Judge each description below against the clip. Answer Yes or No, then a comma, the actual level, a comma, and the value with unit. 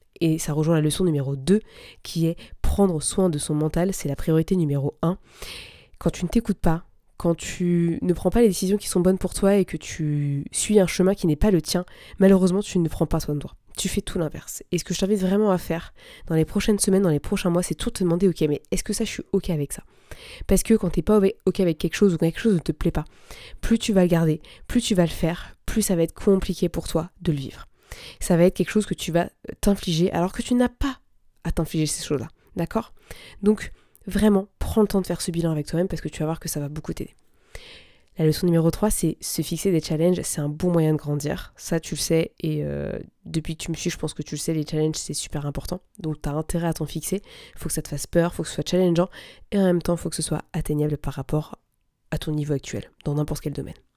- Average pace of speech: No, fast, 270 wpm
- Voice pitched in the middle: Yes, medium, 170 Hz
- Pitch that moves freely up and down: No, average, 3.6 semitones